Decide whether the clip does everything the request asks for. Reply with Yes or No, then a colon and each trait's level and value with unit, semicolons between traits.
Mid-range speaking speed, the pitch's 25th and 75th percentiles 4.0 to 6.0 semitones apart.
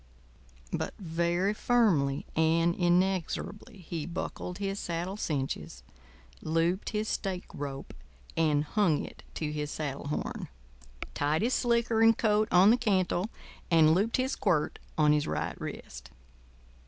No: slow, 130 wpm; average, 5.2 semitones